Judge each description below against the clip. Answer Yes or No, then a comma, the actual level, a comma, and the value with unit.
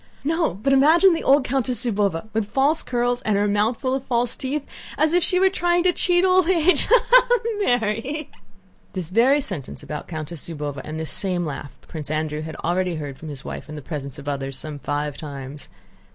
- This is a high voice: Yes, high, 215 Hz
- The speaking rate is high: Yes, fast, 210 wpm